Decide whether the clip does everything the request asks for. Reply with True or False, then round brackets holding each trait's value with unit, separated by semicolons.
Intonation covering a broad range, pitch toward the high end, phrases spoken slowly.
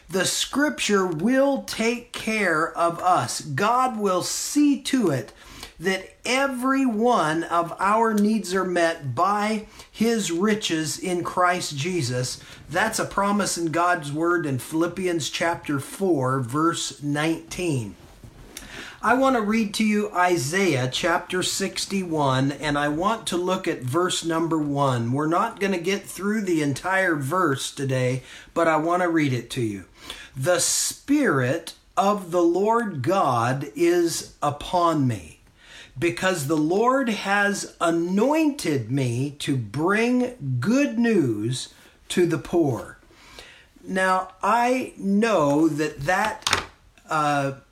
False (5.8 semitones; 175 Hz; 130 wpm)